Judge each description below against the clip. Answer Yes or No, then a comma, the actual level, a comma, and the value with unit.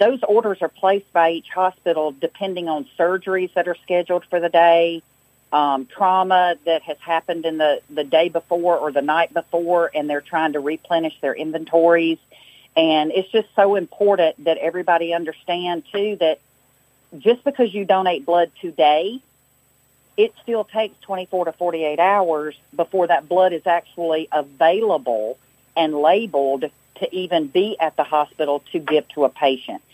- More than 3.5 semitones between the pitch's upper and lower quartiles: No, average, 3.0 semitones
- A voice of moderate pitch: Yes, medium, 165 Hz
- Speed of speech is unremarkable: Yes, average, 160 wpm